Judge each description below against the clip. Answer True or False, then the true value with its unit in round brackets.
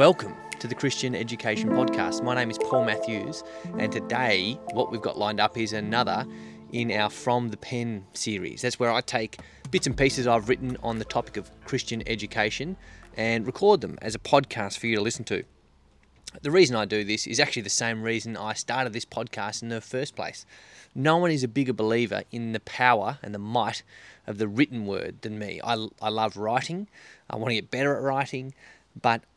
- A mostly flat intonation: False (3.0 semitones)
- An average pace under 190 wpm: False (205 wpm)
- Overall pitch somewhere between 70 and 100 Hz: False (115 Hz)